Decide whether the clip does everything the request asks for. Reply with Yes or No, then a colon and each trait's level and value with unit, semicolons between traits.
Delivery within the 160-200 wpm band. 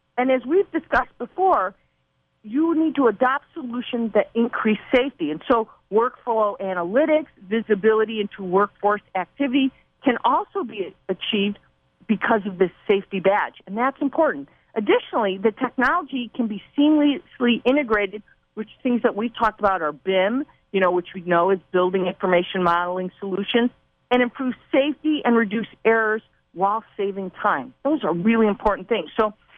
No: average, 150 wpm